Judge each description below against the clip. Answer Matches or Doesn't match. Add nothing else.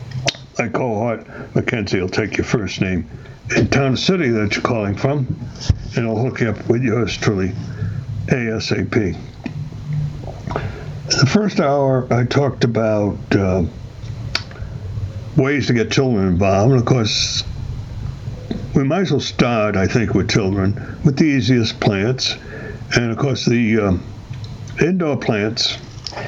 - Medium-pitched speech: Doesn't match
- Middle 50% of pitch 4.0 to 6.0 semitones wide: Doesn't match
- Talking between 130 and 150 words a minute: Matches